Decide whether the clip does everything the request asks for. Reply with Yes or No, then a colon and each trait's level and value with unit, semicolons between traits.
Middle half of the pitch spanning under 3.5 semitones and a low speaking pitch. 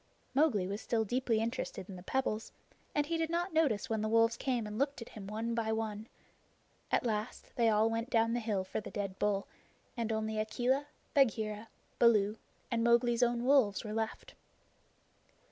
No: narrow, 2.4 semitones; high, 225 Hz